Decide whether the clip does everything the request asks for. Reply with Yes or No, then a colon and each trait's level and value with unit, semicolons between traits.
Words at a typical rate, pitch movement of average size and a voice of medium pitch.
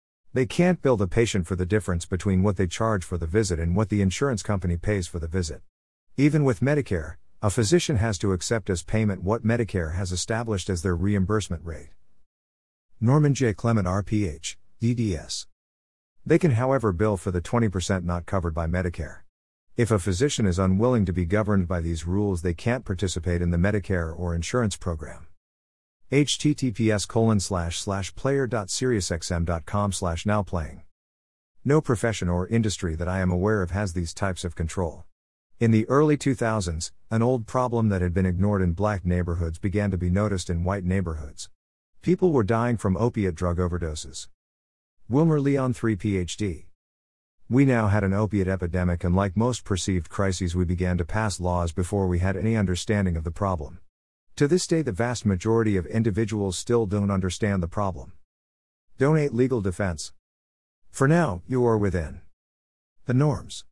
No: average, 160 wpm; average, 4.4 semitones; very low, 95 Hz